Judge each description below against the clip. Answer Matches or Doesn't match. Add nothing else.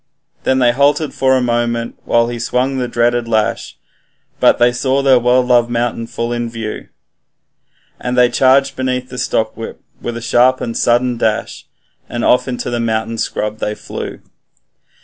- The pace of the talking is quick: Doesn't match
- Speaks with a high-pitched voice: Doesn't match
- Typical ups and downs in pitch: Doesn't match